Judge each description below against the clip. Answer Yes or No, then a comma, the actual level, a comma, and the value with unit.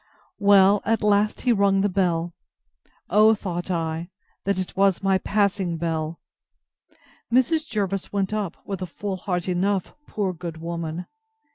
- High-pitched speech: Yes, high, 195 Hz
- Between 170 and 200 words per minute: No, average, 145 wpm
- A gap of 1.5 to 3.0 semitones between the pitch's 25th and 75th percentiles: Yes, average, 2.7 semitones